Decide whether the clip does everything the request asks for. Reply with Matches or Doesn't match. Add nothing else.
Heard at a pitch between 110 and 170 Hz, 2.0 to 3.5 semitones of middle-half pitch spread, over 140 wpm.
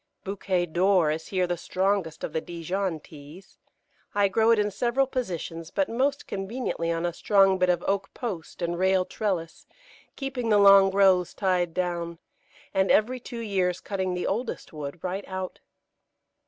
Doesn't match